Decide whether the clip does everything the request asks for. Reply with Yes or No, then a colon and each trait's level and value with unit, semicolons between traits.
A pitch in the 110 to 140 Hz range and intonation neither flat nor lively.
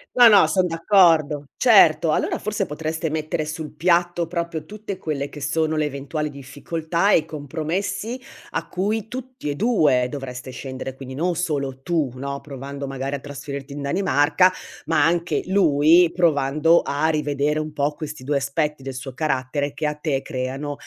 No: medium, 150 Hz; average, 3.3 semitones